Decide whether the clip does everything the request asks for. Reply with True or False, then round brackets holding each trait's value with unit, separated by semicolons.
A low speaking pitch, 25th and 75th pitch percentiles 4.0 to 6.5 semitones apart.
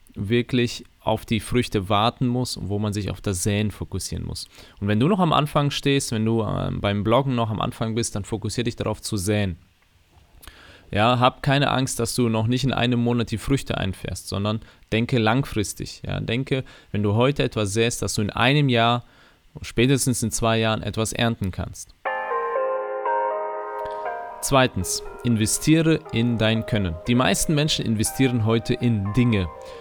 False (115 Hz; 3.2 semitones)